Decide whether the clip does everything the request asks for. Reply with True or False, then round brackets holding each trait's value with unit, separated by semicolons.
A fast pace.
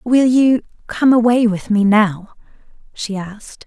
False (145 wpm)